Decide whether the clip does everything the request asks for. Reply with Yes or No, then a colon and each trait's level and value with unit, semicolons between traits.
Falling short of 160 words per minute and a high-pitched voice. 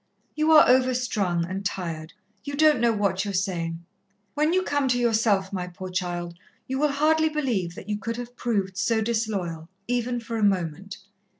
No: average, 185 wpm; high, 215 Hz